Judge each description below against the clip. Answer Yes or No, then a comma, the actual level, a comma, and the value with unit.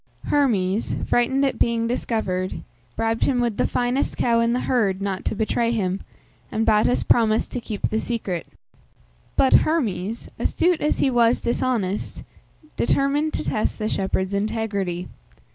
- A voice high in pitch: Yes, high, 225 Hz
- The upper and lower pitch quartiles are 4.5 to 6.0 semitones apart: No, average, 3.6 semitones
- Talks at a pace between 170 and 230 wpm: No, average, 145 wpm